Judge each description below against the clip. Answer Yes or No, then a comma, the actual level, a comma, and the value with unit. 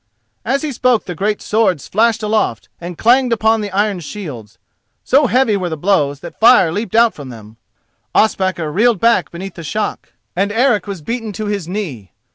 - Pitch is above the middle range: Yes, high, 205 Hz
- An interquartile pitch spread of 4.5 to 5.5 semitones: Yes, average, 4.9 semitones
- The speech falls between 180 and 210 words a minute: Yes, average, 185 wpm